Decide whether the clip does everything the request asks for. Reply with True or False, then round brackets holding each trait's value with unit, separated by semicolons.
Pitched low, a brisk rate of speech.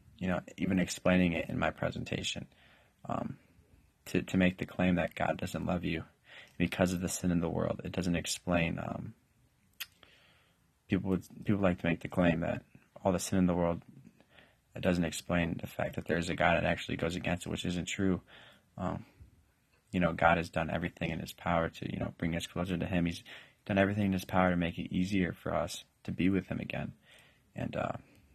True (90 Hz; 210 wpm)